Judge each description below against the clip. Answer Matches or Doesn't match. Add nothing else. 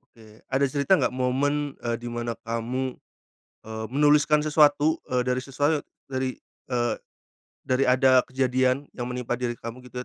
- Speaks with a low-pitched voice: Matches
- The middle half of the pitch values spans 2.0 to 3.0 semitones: Matches